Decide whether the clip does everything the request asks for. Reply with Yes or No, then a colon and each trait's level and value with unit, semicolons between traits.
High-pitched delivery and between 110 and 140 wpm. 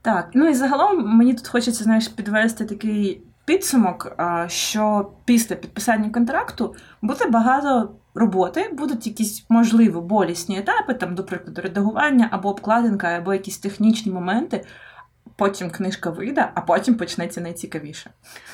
Yes: high, 215 Hz; average, 130 wpm